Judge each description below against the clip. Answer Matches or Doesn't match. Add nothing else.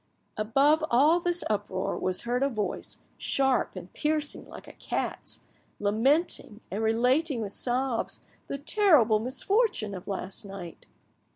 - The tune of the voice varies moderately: Doesn't match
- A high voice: Matches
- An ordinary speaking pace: Doesn't match